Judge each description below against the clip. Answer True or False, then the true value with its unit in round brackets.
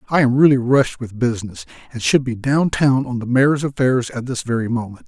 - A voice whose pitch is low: True (125 Hz)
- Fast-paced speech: True (225 wpm)